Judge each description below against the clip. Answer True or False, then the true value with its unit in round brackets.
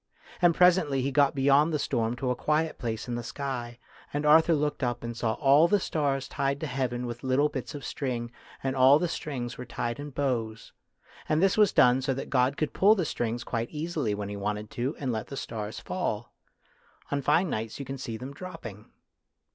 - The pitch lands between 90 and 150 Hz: True (135 Hz)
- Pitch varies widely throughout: False (3.8 semitones)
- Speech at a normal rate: False (210 wpm)